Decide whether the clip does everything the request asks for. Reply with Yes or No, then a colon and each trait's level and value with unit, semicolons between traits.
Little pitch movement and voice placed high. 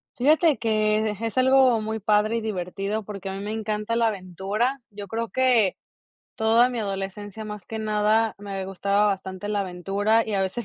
Yes: narrow, 2.3 semitones; high, 215 Hz